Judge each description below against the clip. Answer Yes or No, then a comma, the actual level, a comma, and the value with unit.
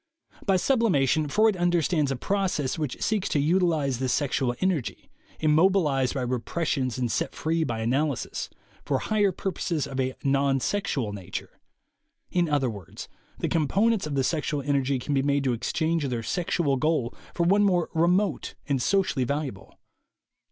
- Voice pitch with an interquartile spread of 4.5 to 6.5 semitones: Yes, average, 5.0 semitones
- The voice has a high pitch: No, medium, 150 Hz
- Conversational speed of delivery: Yes, average, 160 wpm